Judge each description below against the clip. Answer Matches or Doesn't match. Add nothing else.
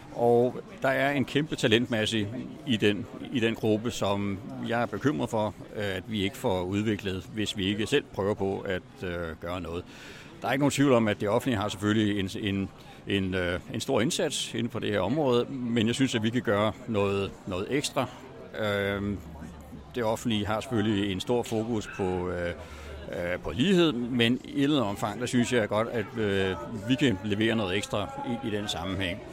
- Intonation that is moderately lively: Matches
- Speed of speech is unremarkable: Matches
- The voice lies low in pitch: Matches